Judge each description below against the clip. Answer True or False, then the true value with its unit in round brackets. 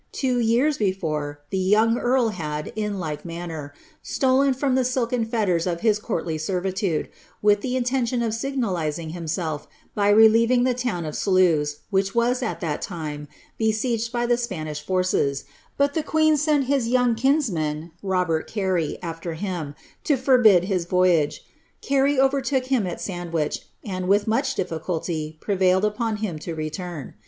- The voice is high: True (200 Hz)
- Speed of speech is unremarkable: True (155 wpm)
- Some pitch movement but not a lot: False (6.6 semitones)